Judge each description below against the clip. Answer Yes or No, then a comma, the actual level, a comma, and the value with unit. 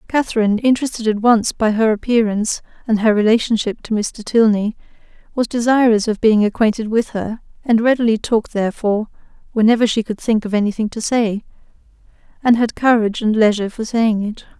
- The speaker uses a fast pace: No, average, 165 wpm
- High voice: Yes, high, 220 Hz